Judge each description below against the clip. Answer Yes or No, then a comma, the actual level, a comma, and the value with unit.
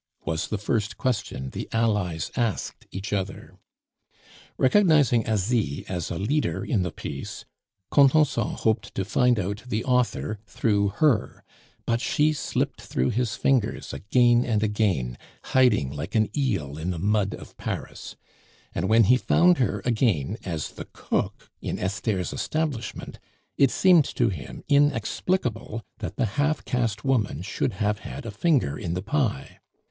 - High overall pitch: No, low, 110 Hz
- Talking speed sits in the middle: Yes, average, 150 wpm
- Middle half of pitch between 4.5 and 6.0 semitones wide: Yes, average, 4.8 semitones